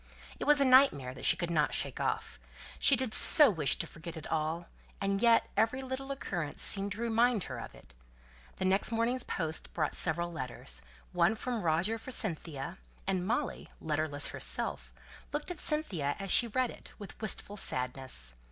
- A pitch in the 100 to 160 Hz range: No, high, 195 Hz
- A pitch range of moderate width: No, wide, 7.5 semitones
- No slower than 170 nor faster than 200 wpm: Yes, average, 180 wpm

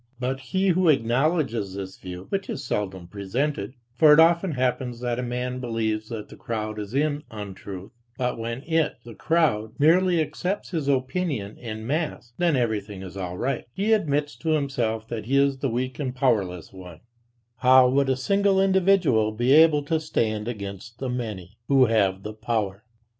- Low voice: Yes, low, 125 Hz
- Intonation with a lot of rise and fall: Yes, wide, 5.7 semitones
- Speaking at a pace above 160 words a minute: Yes, average, 175 wpm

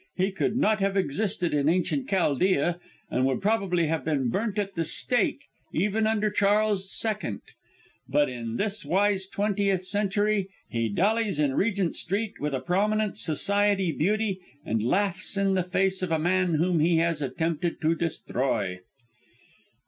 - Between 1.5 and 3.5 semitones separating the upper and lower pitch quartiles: No, average, 4.3 semitones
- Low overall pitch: No, medium, 185 Hz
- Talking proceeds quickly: No, average, 155 wpm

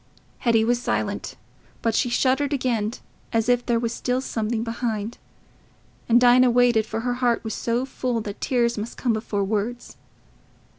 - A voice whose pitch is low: No, high, 235 Hz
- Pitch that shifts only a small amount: Yes, narrow, 1.7 semitones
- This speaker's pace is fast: No, average, 160 wpm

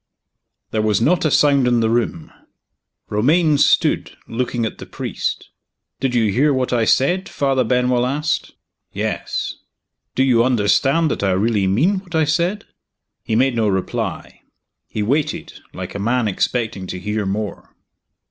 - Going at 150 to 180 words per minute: Yes, average, 155 wpm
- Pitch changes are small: No, average, 4.7 semitones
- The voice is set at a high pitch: No, low, 125 Hz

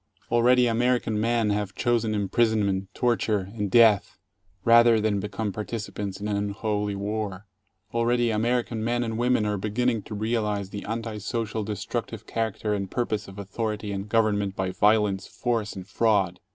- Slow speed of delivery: No, average, 155 wpm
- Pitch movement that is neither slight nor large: No, narrow, 2.2 semitones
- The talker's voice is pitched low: Yes, low, 110 Hz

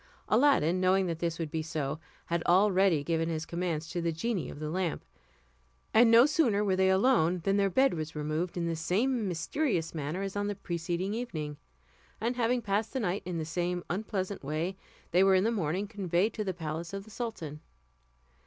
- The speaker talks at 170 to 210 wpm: Yes, average, 200 wpm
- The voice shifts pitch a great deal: No, average, 4.0 semitones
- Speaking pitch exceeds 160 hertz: Yes, medium, 185 Hz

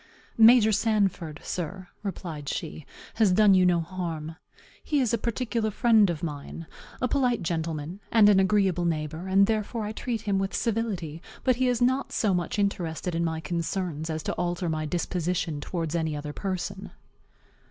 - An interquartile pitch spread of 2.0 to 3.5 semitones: No, average, 4.7 semitones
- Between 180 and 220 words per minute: No, average, 170 wpm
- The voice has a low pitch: No, medium, 185 Hz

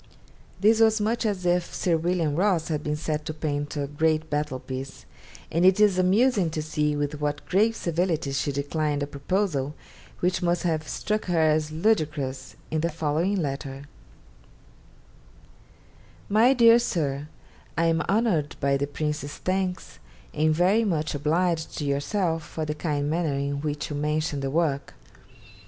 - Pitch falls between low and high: Yes, medium, 155 Hz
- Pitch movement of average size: Yes, average, 3.8 semitones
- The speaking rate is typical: Yes, average, 160 wpm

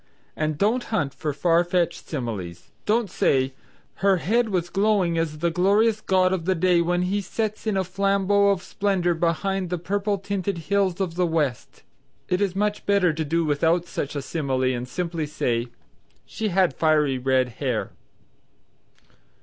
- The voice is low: No, medium, 175 Hz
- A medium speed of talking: Yes, average, 160 wpm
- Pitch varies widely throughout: No, average, 4.4 semitones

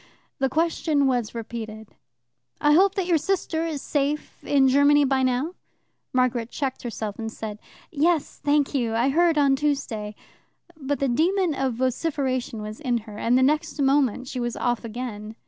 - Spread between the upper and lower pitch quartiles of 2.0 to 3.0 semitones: No, average, 3.9 semitones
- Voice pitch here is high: Yes, very high, 270 Hz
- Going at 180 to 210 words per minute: No, average, 165 wpm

